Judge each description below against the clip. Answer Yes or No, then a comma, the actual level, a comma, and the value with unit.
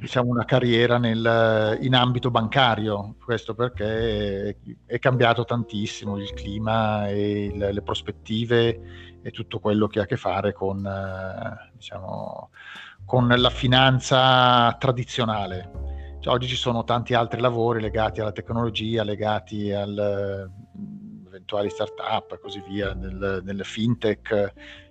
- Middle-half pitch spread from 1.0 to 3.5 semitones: Yes, average, 2.9 semitones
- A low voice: Yes, low, 110 Hz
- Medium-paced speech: Yes, average, 130 wpm